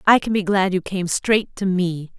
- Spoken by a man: No, female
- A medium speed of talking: No, fast, 245 wpm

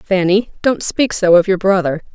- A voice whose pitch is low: No, high, 190 Hz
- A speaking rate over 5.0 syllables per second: No, 4.7 syllables/s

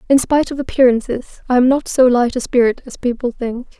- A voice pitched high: Yes, very high, 250 Hz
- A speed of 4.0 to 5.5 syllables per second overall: No, 5.9 syllables/s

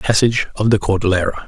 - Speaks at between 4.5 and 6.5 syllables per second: No, 6.7 syllables/s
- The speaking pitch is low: Yes, low, 100 Hz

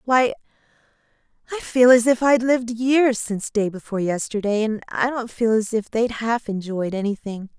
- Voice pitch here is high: Yes, high, 225 Hz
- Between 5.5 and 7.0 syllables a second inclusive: No, 5.0 syllables/s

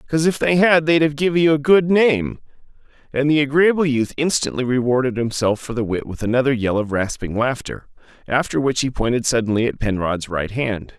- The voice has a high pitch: No, low, 135 Hz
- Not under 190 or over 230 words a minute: Yes, average, 195 wpm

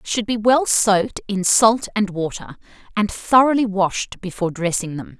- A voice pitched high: Yes, high, 205 Hz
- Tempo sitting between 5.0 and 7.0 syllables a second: No, 4.6 syllables/s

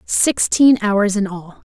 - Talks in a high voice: Yes, high, 205 Hz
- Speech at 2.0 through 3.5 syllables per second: Yes, 3.3 syllables/s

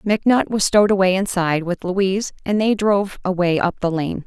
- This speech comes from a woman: Yes, female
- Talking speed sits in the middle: Yes, average, 195 wpm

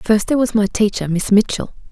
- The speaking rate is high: Yes, fast, 220 wpm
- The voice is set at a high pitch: Yes, high, 210 Hz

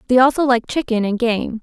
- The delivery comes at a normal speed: No, fast, 220 wpm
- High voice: Yes, high, 240 Hz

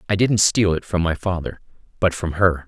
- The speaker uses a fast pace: Yes, fast, 225 wpm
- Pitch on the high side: No, very low, 90 Hz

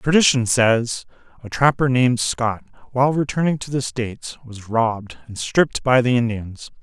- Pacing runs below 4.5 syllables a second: No, 4.9 syllables/s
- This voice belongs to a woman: No, male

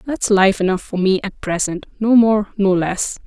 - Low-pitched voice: No, high, 200 Hz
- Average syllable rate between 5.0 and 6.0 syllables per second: No, 4.6 syllables/s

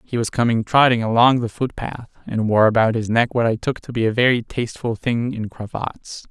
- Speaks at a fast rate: Yes, fast, 230 wpm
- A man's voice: Yes, male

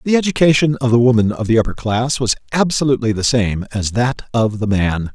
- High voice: No, low, 120 Hz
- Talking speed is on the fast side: Yes, fast, 210 wpm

